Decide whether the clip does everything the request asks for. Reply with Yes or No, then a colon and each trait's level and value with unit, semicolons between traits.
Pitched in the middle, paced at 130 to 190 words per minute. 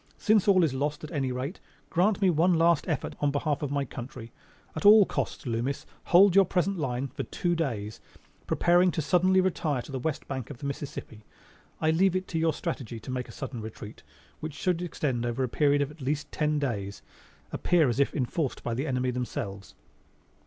No: medium, 145 Hz; average, 200 wpm